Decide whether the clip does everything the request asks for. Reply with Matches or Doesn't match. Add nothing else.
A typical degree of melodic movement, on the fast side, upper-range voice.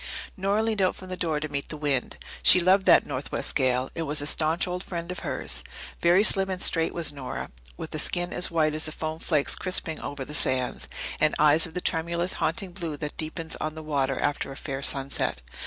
Doesn't match